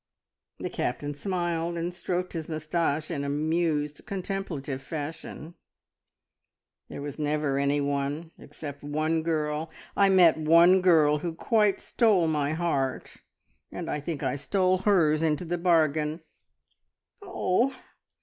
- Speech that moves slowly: Yes, slow, 120 wpm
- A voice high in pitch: No, medium, 160 Hz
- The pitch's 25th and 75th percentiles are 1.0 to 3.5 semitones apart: Yes, average, 3.0 semitones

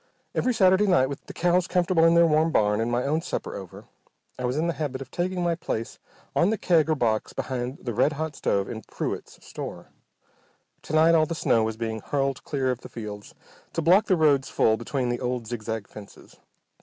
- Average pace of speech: No, fast, 215 wpm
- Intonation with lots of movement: Yes, wide, 5.9 semitones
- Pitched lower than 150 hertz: Yes, medium, 140 Hz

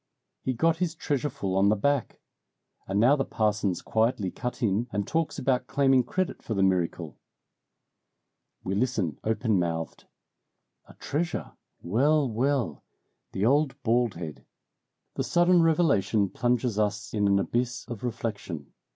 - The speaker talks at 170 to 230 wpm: No, average, 140 wpm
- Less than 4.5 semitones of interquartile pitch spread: No, wide, 5.6 semitones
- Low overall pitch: Yes, low, 115 Hz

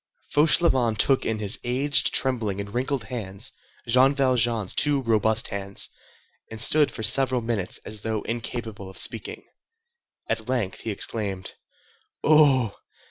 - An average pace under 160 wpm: Yes, slow, 135 wpm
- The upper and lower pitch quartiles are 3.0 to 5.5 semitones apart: Yes, average, 3.8 semitones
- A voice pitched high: No, low, 115 Hz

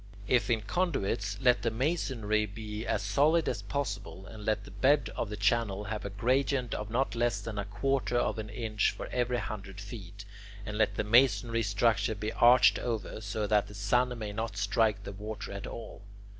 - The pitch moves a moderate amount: Yes, average, 3.0 semitones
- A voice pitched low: Yes, low, 110 Hz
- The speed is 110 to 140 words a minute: No, average, 195 wpm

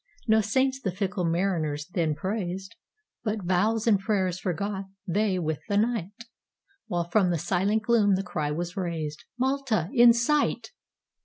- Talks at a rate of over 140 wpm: No, slow, 135 wpm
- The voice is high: Yes, high, 195 Hz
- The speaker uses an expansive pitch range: No, average, 4.2 semitones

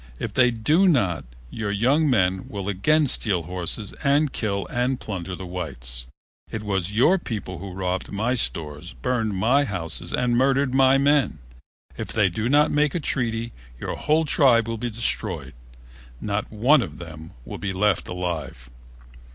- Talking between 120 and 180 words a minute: Yes, average, 165 wpm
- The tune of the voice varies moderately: No, wide, 6.1 semitones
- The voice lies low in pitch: Yes, low, 110 Hz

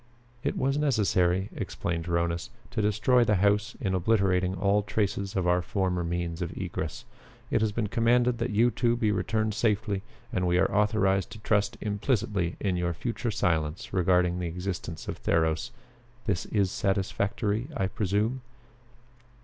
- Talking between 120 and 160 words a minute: Yes, average, 155 wpm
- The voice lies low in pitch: Yes, low, 100 Hz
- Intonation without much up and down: No, average, 3.3 semitones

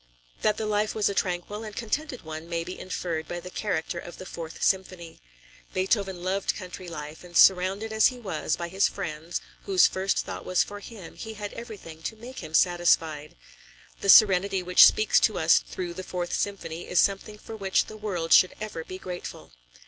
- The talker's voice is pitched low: No, medium, 185 Hz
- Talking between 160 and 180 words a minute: No, average, 195 wpm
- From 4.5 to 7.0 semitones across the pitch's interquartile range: No, average, 3.3 semitones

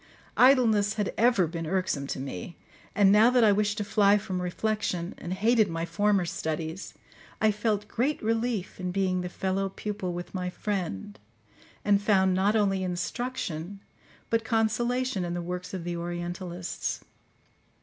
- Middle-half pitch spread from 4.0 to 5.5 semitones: No, average, 3.4 semitones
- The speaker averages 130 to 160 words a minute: Yes, average, 155 wpm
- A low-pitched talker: No, high, 195 Hz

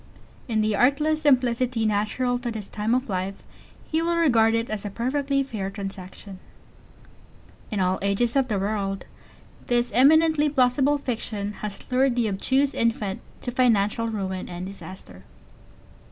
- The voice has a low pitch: No, high, 230 Hz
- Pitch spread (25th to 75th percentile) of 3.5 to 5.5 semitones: Yes, average, 4.6 semitones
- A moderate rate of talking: Yes, average, 145 wpm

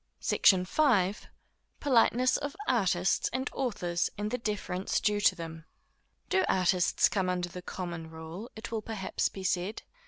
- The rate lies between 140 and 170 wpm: Yes, average, 150 wpm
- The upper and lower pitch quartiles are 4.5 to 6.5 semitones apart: No, average, 4.1 semitones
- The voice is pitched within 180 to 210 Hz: Yes, high, 190 Hz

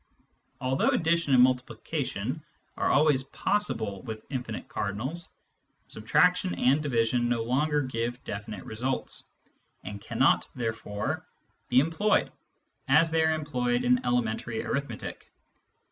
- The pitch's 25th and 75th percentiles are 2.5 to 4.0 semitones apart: No, average, 4.5 semitones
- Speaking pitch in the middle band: No, low, 125 Hz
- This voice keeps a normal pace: No, slow, 115 wpm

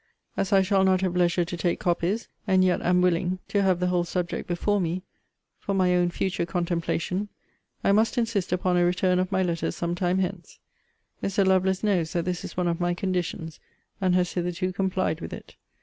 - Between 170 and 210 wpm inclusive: Yes, average, 200 wpm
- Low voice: No, medium, 180 Hz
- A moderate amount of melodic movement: No, narrow, 1.4 semitones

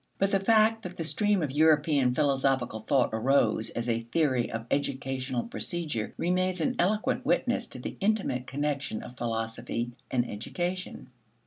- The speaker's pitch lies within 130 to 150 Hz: Yes, medium, 140 Hz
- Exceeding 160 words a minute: No, average, 150 wpm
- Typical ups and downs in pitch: No, wide, 6.5 semitones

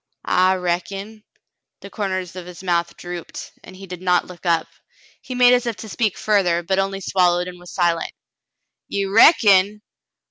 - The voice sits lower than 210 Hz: Yes, medium, 185 Hz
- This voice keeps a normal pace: Yes, average, 170 wpm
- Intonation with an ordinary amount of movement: No, narrow, 2.3 semitones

